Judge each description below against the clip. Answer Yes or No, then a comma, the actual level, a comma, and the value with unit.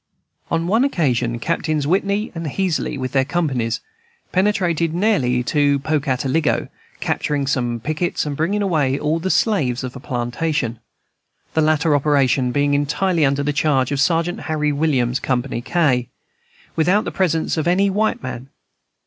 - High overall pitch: No, medium, 150 Hz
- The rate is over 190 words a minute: No, average, 150 wpm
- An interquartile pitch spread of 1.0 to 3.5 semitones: No, average, 4.3 semitones